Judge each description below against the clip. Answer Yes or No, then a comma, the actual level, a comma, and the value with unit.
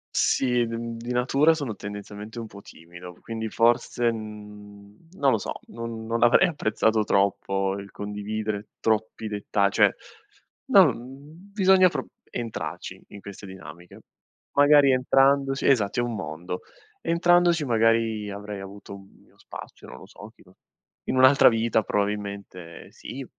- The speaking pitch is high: No, low, 110 Hz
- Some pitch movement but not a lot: Yes, average, 4.0 semitones